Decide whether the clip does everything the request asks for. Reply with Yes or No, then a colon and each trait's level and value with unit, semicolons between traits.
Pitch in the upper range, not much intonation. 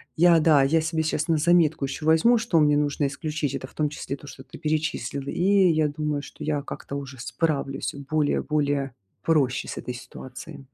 No: medium, 150 Hz; narrow, 2.2 semitones